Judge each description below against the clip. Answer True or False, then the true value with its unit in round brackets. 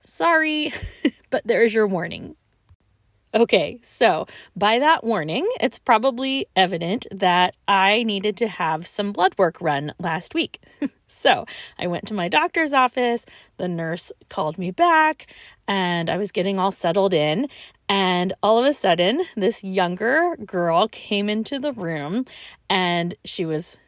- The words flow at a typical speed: True (145 wpm)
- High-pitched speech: True (195 Hz)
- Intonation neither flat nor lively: False (5.7 semitones)